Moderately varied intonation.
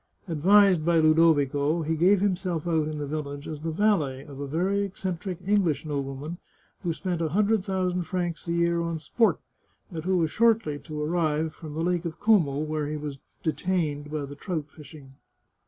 Yes: average, 3.3 semitones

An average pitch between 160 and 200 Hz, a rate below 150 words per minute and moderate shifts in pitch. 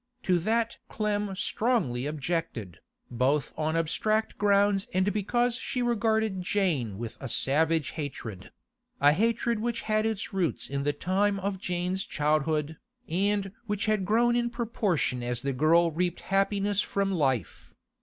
No: high, 190 Hz; average, 140 wpm; wide, 5.9 semitones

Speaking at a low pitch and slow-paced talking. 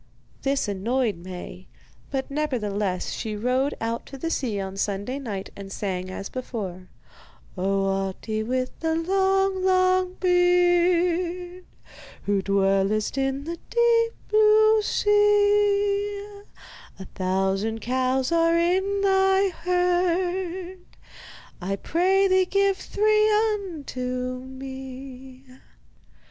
No: very high, 285 Hz; slow, 105 wpm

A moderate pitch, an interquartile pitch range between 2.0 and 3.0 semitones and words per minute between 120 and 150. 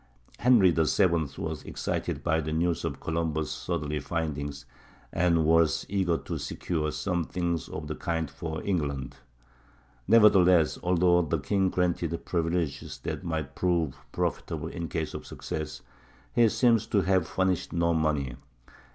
No: very low, 85 Hz; narrow, 2.5 semitones; slow, 135 wpm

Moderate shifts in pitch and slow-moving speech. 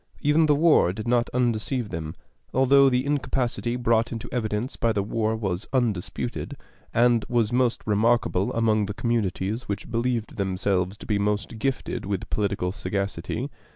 No: average, 3.3 semitones; average, 155 wpm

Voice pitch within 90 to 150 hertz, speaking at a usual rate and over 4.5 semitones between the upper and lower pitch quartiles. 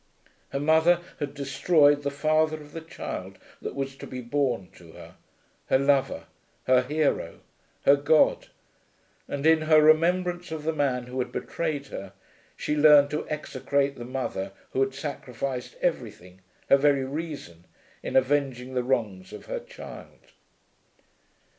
No: medium, 140 Hz; average, 145 wpm; average, 3.3 semitones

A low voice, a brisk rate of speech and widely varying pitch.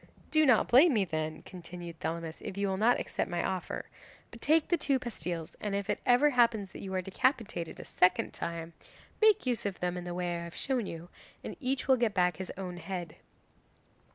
No: high, 190 Hz; fast, 210 wpm; wide, 5.9 semitones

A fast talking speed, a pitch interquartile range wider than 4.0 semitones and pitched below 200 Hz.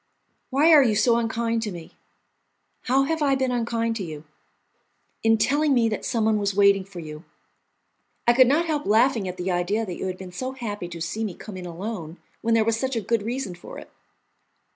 No: fast, 210 wpm; average, 4.8 semitones; high, 225 Hz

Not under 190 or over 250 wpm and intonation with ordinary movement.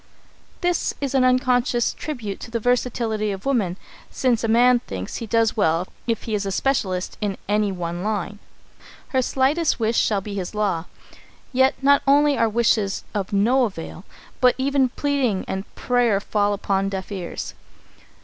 No: average, 165 wpm; average, 4.3 semitones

